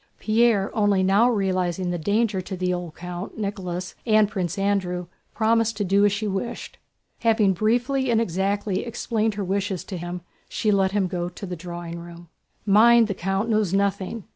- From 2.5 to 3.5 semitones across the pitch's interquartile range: Yes, average, 3.0 semitones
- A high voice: Yes, high, 195 Hz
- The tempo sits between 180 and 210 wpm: No, average, 165 wpm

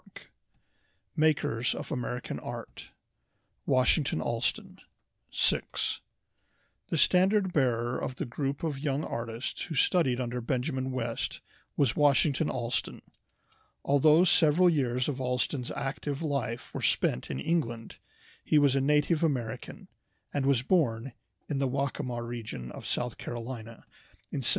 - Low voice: Yes, low, 130 Hz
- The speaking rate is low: Yes, slow, 130 wpm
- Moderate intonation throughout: Yes, average, 3.6 semitones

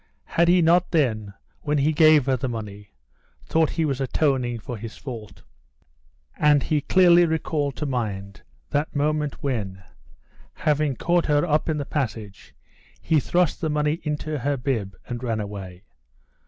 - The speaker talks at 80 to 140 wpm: No, average, 155 wpm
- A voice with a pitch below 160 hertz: Yes, medium, 140 Hz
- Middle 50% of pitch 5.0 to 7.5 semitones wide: Yes, average, 5.3 semitones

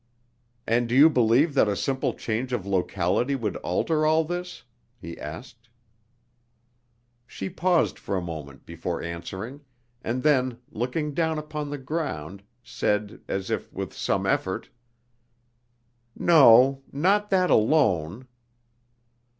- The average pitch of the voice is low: Yes, low, 125 Hz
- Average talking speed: No, slow, 125 wpm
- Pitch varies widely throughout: Yes, wide, 7.4 semitones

